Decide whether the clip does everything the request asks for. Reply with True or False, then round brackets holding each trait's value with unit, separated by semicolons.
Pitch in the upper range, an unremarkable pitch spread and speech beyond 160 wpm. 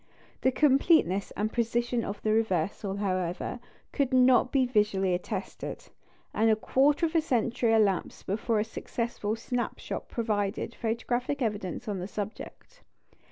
False (225 Hz; 3.5 semitones; 140 wpm)